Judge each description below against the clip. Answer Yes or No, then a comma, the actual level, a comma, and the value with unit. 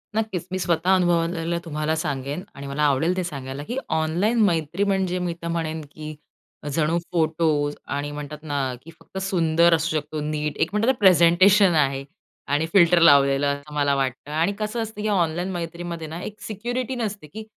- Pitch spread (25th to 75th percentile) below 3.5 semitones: No, average, 3.8 semitones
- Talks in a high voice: No, medium, 165 Hz